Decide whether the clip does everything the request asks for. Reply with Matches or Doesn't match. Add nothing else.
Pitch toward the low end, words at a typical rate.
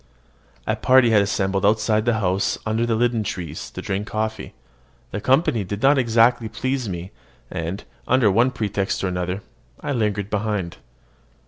Matches